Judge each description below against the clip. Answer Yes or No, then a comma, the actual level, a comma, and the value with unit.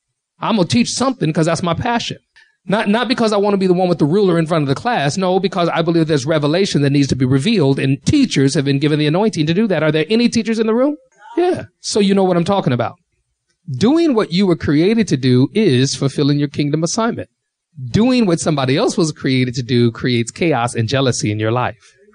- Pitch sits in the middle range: Yes, medium, 165 Hz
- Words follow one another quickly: Yes, fast, 240 wpm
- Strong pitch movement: Yes, wide, 6.9 semitones